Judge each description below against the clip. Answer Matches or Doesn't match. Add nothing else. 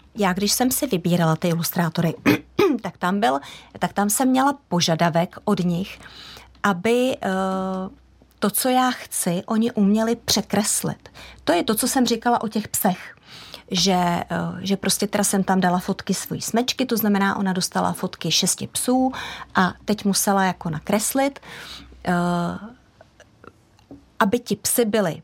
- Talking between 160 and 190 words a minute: Doesn't match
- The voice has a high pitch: Matches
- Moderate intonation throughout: Matches